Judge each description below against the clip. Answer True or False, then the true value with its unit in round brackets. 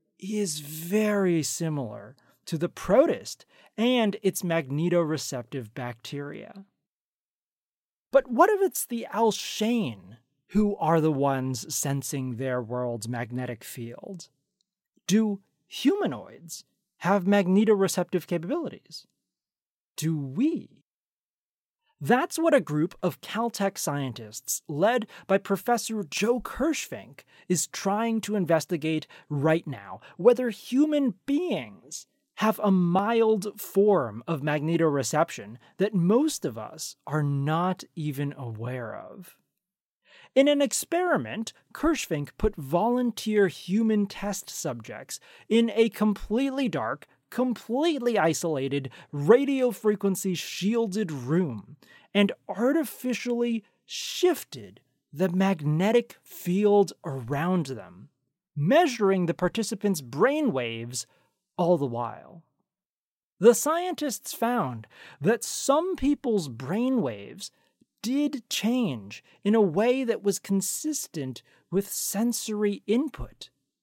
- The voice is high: True (195 Hz)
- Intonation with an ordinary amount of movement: False (7.3 semitones)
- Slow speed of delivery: True (100 wpm)